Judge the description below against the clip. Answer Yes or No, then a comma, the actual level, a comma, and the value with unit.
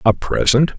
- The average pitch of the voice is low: Yes, low, 125 Hz